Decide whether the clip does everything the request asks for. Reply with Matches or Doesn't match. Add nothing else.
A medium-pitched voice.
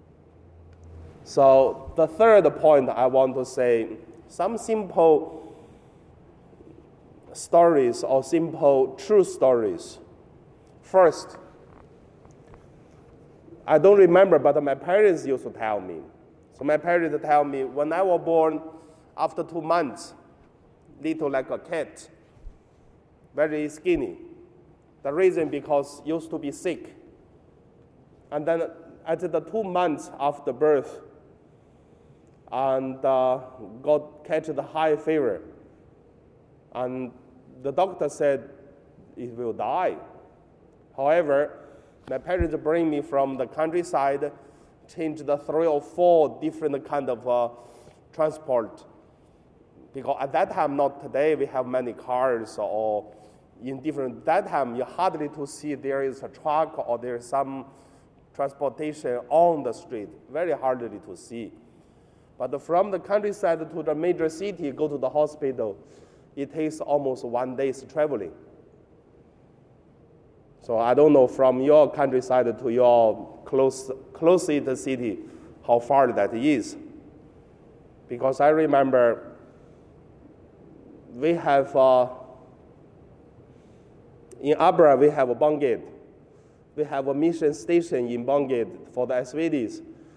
Matches